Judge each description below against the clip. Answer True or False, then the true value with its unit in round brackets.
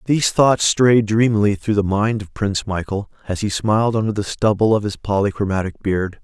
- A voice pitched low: True (105 Hz)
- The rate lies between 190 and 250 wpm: True (195 wpm)